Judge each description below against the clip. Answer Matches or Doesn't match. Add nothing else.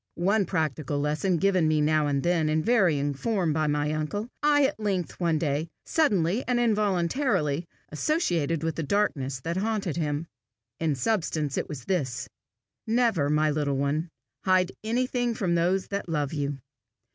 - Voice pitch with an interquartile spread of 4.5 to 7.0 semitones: Matches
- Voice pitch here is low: Doesn't match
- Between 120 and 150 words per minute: Doesn't match